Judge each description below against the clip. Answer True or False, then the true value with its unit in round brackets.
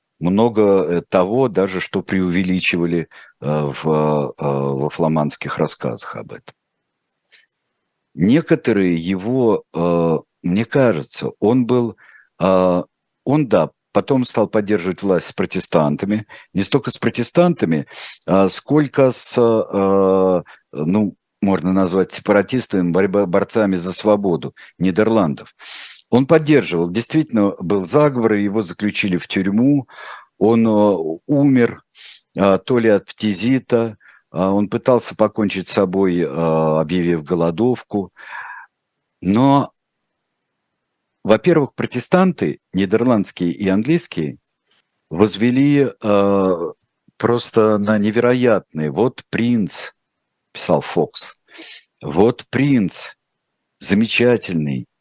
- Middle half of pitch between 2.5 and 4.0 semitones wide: False (4.6 semitones)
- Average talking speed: False (85 wpm)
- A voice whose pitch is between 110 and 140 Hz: False (100 Hz)